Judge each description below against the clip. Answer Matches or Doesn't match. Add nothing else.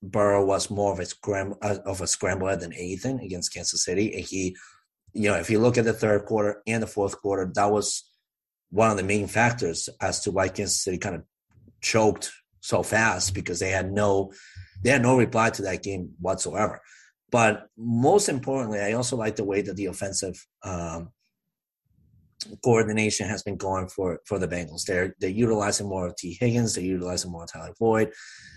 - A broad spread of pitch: Doesn't match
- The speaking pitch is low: Matches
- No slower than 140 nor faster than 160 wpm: Doesn't match